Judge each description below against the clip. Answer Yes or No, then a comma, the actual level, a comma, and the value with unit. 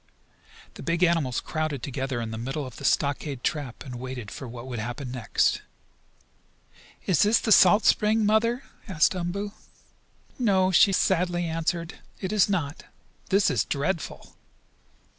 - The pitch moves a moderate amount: No, wide, 6.5 semitones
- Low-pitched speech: No, medium, 160 Hz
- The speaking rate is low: No, average, 145 wpm